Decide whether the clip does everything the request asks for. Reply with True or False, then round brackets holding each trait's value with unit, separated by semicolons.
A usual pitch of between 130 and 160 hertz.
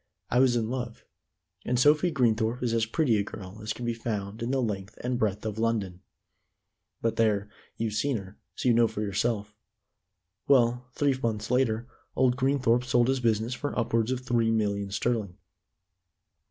False (115 Hz)